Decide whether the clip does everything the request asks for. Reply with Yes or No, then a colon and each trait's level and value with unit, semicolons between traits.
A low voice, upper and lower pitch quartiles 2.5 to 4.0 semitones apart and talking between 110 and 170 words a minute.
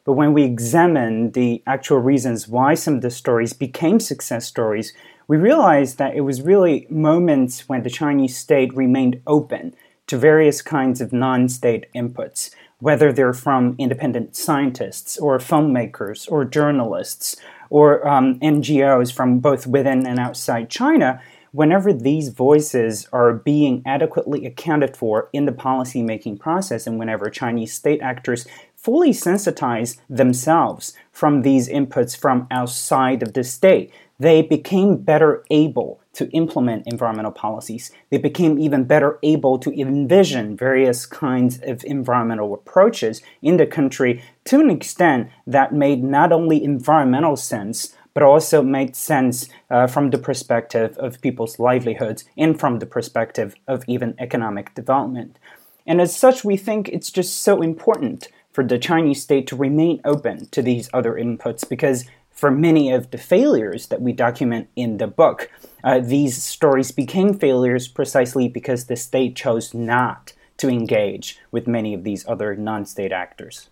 Yes: low, 130 Hz; average, 3.5 semitones; average, 150 wpm